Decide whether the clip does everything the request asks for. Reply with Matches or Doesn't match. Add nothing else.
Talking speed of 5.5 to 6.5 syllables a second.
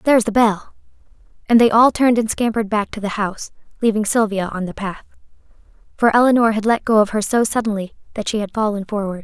Matches